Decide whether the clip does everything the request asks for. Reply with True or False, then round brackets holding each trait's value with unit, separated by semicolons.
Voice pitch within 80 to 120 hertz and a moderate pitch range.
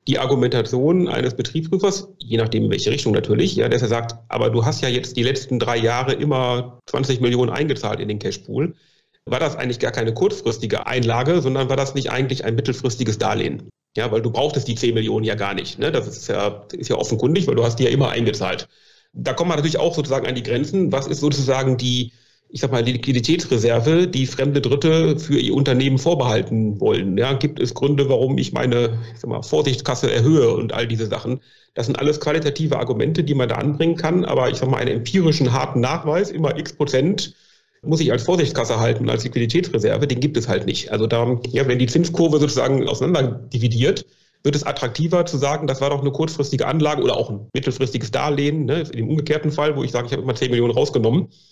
False (135 Hz; 3.5 semitones)